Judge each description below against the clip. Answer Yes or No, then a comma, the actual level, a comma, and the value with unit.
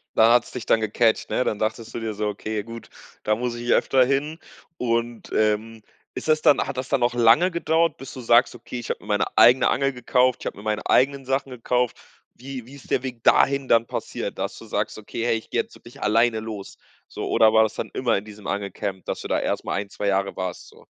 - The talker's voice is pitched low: Yes, low, 115 Hz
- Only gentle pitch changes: No, average, 3.0 semitones